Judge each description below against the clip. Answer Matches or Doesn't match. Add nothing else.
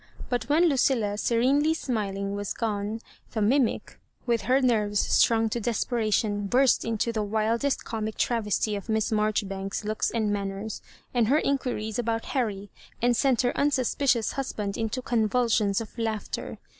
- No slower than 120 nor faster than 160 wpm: Matches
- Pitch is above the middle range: Matches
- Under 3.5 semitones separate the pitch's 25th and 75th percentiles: Matches